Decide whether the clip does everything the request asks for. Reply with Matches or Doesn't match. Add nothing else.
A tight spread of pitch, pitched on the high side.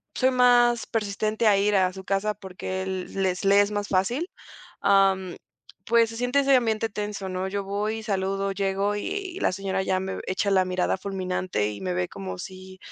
Matches